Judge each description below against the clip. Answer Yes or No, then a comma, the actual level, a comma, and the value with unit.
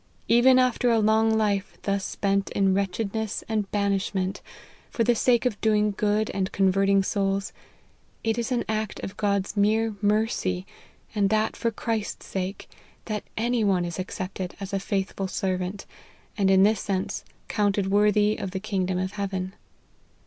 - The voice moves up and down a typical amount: No, narrow, 2.1 semitones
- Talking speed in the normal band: Yes, average, 160 wpm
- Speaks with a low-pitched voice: No, high, 200 Hz